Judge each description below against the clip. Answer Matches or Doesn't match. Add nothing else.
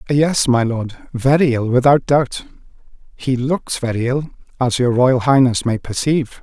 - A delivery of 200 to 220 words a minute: Doesn't match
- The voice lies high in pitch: Doesn't match